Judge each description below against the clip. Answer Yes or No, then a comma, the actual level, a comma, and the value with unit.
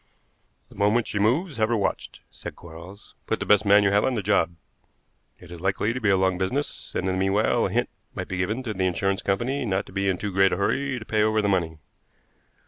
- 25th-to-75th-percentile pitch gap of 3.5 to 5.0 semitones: No, narrow, 2.6 semitones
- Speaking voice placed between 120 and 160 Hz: No, low, 100 Hz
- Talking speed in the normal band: No, fast, 250 wpm